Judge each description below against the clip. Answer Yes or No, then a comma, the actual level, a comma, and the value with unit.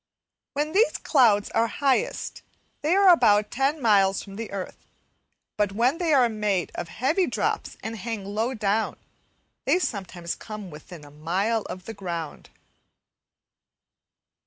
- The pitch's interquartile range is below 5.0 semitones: No, average, 5.3 semitones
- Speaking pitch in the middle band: No, high, 215 Hz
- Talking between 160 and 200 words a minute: No, average, 140 wpm